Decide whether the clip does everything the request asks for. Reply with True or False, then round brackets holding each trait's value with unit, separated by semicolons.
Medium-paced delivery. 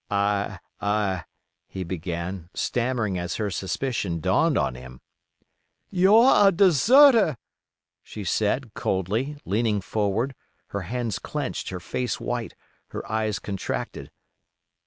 False (110 wpm)